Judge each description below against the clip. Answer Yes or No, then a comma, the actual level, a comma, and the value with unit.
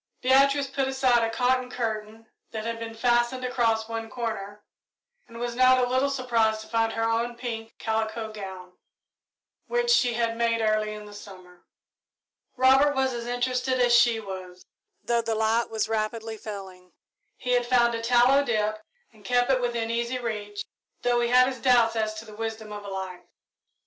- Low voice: No, high, 230 Hz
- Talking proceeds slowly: No, average, 180 wpm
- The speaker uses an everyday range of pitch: No, narrow, 2.3 semitones